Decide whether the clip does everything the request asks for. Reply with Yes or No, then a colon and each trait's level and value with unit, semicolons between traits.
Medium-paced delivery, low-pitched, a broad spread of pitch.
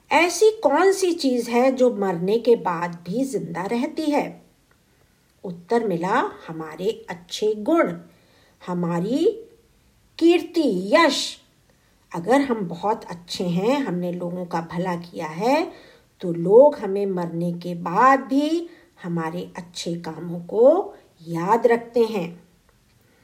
No: average, 120 wpm; high, 215 Hz; wide, 8.4 semitones